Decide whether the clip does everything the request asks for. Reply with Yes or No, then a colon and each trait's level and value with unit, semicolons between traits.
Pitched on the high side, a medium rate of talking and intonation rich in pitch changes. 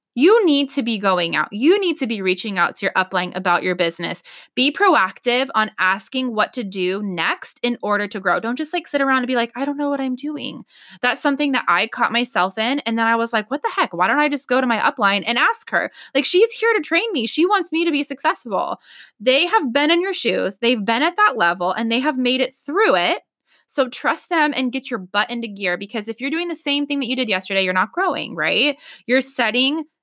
No: very high, 255 Hz; fast, 250 wpm; wide, 5.8 semitones